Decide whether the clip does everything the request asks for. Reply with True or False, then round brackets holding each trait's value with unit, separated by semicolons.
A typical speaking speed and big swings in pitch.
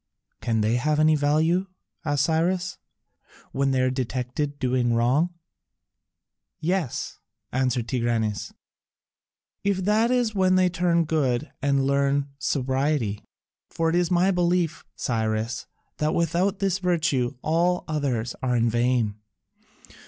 False (125 wpm; 5.9 semitones)